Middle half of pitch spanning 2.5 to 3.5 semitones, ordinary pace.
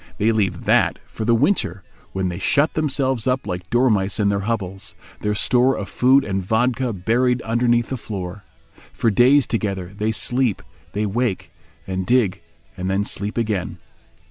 No: average, 4.2 semitones; average, 160 wpm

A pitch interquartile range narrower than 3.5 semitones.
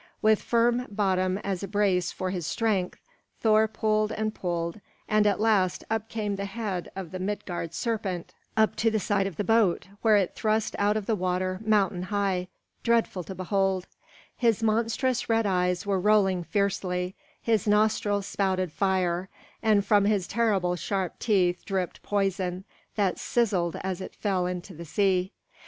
Yes: average, 2.8 semitones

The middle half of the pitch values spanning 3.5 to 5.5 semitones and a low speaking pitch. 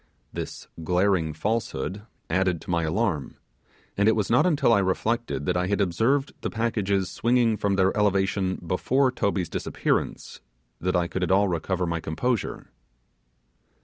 Yes: average, 3.9 semitones; very low, 95 Hz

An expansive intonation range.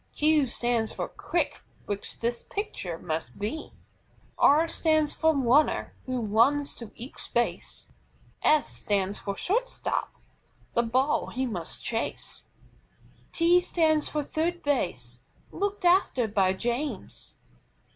Yes: wide, 6.5 semitones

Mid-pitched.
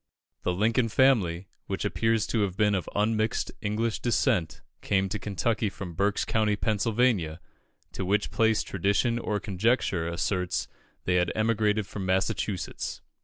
No: low, 105 Hz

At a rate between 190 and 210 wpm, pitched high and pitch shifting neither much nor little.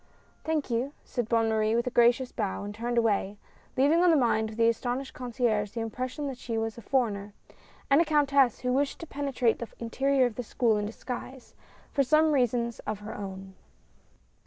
Yes: average, 195 wpm; high, 240 Hz; average, 3.5 semitones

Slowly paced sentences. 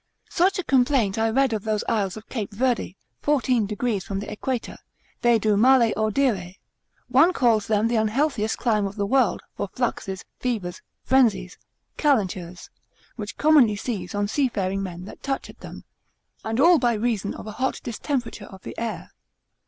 No: average, 170 wpm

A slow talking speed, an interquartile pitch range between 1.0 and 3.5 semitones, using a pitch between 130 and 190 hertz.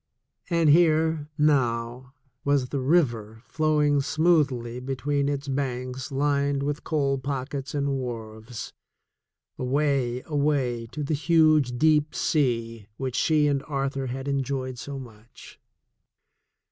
Yes: slow, 120 wpm; average, 2.8 semitones; medium, 140 Hz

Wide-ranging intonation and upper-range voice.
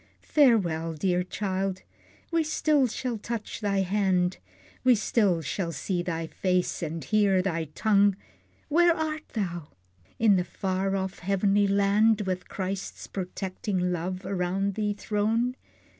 No: average, 2.9 semitones; high, 195 Hz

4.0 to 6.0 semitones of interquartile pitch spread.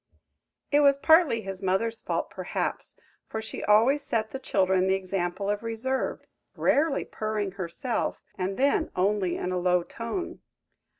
Yes: wide, 5.6 semitones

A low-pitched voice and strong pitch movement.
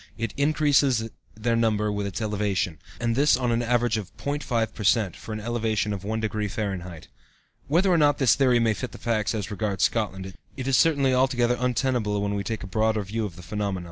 No: low, 110 Hz; average, 3.2 semitones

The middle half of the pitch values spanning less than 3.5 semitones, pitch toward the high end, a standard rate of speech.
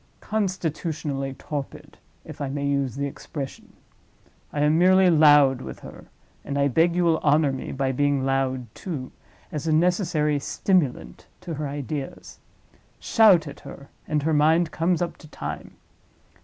No: average, 3.0 semitones; medium, 150 Hz; average, 145 wpm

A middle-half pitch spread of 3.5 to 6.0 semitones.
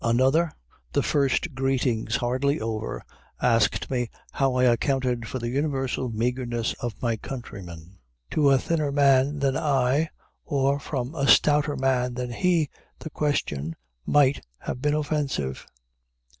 No: average, 3.1 semitones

